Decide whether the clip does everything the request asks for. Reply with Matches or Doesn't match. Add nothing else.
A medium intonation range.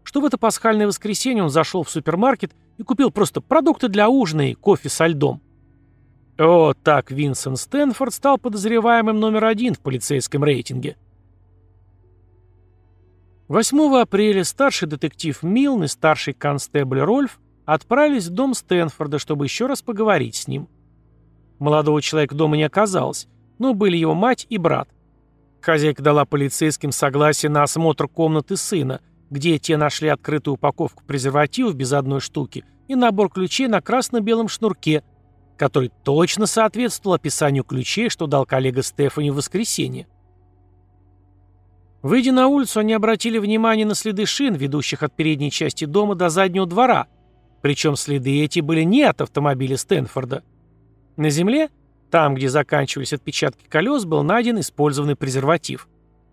Doesn't match